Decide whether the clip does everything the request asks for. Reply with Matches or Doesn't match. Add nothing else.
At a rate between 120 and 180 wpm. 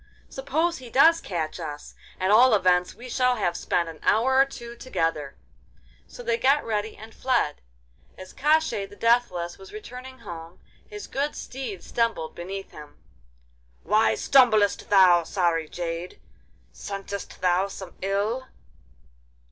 Matches